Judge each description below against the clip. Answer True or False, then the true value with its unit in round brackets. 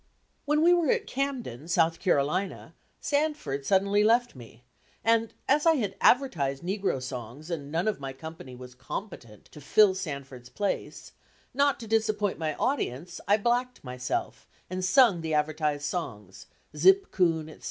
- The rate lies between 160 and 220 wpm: False (150 wpm)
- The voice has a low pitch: False (175 Hz)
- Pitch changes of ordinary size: False (8.0 semitones)